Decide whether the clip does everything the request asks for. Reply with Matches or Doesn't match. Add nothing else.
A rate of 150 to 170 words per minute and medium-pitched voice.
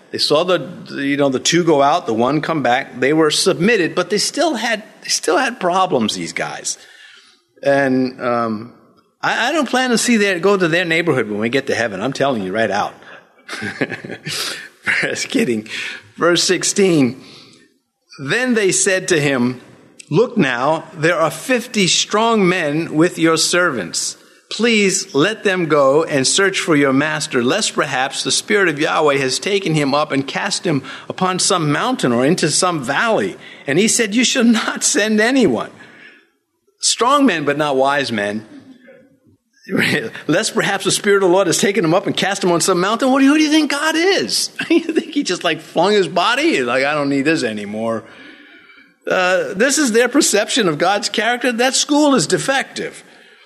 Doesn't match